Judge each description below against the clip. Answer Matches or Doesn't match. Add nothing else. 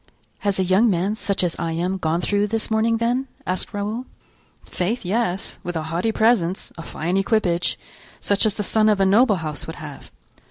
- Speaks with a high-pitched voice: Matches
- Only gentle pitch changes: Doesn't match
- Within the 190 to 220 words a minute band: Matches